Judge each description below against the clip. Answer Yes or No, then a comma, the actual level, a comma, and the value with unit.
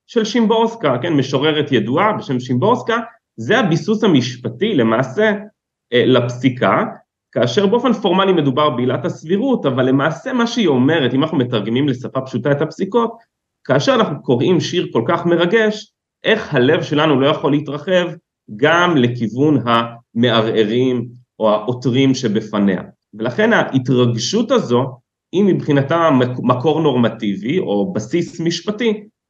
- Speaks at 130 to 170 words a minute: No, average, 120 wpm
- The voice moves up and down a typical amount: No, wide, 7.5 semitones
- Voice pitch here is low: No, medium, 145 Hz